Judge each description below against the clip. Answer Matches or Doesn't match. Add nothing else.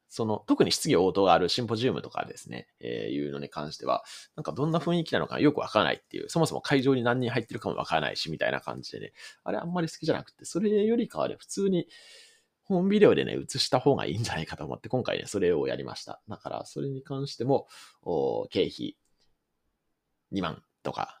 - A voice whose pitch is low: Doesn't match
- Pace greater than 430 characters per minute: Matches